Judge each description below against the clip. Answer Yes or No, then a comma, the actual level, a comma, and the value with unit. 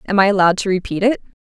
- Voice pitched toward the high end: Yes, high, 195 Hz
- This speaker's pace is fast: Yes, fast, 255 wpm